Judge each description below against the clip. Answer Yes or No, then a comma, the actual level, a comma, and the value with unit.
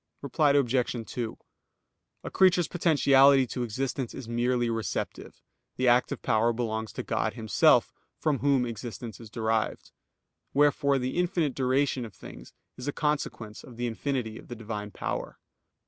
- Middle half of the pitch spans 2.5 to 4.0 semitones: Yes, average, 3.6 semitones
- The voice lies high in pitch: No, low, 125 Hz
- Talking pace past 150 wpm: No, average, 145 wpm